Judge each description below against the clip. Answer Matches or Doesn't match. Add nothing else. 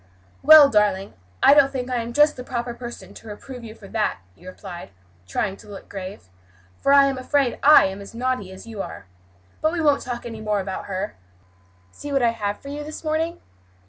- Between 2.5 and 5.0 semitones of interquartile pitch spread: Doesn't match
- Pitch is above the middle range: Matches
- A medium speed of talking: Doesn't match